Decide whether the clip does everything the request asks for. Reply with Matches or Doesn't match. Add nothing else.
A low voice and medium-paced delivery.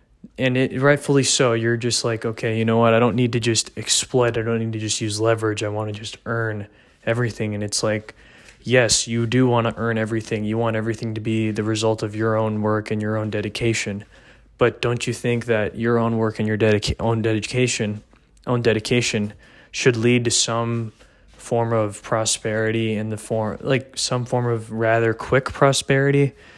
Matches